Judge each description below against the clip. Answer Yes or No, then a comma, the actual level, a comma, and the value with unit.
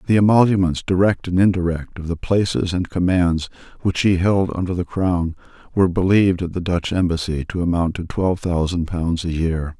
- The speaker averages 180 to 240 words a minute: Yes, average, 185 wpm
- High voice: No, very low, 90 Hz